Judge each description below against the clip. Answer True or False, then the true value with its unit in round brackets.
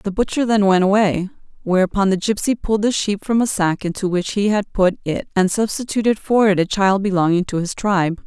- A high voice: True (200 Hz)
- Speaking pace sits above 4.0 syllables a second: True (5.6 syllables/s)